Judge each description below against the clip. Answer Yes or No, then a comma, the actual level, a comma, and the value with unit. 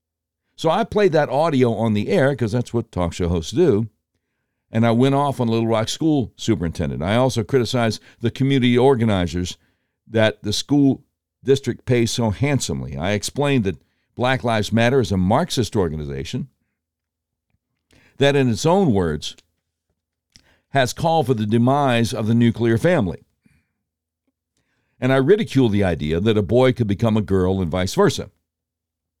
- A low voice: Yes, low, 115 Hz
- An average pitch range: No, wide, 6.5 semitones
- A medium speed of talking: Yes, average, 155 wpm